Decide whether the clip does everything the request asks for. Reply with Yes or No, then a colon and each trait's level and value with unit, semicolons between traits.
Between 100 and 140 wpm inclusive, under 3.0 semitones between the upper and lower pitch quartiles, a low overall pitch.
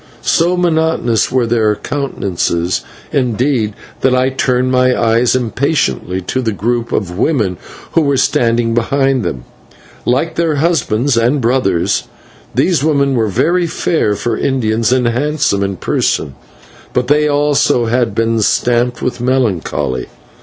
No: slow, 135 wpm; average, 3.8 semitones; low, 125 Hz